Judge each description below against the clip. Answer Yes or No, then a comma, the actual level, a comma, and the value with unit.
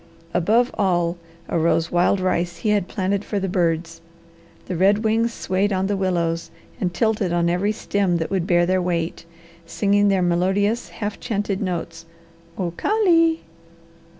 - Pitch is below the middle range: No, medium, 185 Hz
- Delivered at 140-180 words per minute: Yes, average, 155 wpm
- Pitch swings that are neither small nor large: Yes, average, 3.0 semitones